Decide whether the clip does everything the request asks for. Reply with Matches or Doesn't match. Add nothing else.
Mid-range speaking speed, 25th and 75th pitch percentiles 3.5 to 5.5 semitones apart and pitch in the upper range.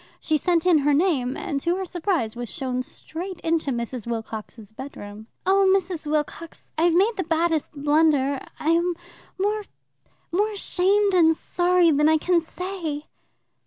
Matches